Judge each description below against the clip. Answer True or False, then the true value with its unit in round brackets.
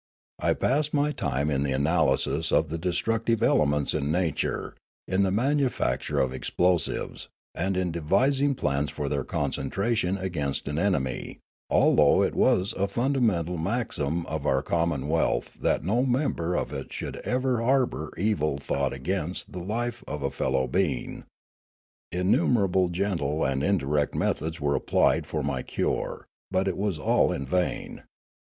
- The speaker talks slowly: False (150 wpm)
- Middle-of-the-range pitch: False (85 Hz)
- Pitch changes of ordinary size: False (5.8 semitones)